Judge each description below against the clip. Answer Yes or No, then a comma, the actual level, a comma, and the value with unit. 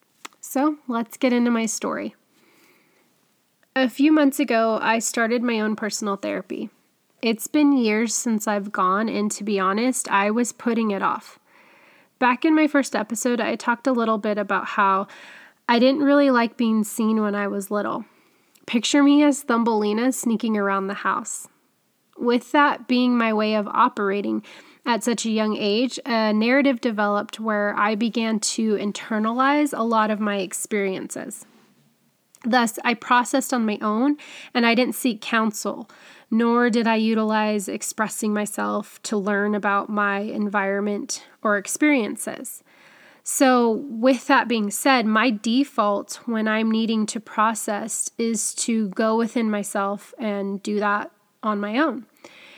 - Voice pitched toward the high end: Yes, high, 225 Hz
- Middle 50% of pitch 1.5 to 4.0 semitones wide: Yes, average, 3.4 semitones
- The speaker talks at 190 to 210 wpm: No, average, 150 wpm